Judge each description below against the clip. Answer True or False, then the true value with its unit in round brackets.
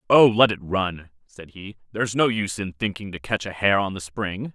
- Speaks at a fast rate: True (240 wpm)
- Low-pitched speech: True (100 Hz)